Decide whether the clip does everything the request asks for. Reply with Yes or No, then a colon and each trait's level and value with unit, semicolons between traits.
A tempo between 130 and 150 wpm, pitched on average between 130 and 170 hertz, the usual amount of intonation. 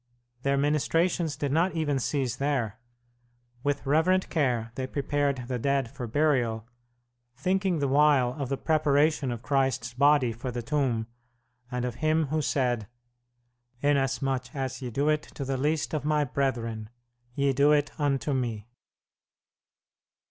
Yes: average, 145 wpm; medium, 140 Hz; average, 3.1 semitones